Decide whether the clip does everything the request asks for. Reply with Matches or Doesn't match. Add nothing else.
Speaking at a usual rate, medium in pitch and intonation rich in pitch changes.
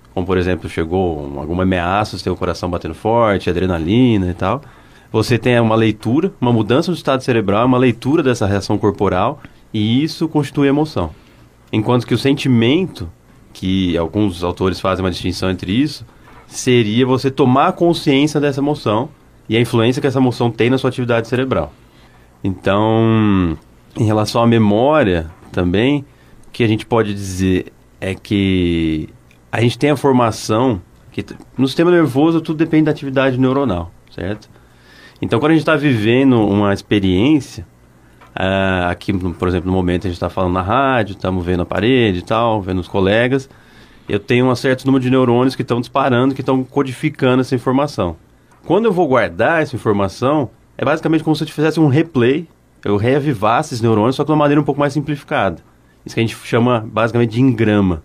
Doesn't match